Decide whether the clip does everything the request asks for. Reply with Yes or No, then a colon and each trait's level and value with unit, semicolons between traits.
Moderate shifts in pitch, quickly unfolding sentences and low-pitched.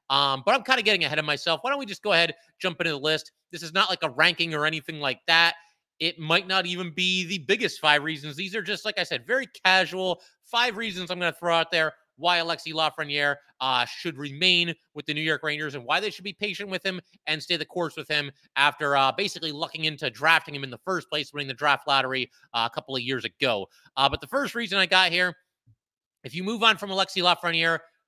No: average, 3.8 semitones; fast, 245 wpm; medium, 165 Hz